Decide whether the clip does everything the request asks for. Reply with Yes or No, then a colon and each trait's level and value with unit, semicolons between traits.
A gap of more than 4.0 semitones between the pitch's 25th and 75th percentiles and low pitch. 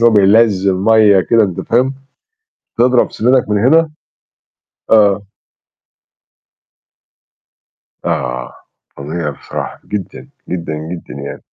Yes: average, 4.6 semitones; low, 105 Hz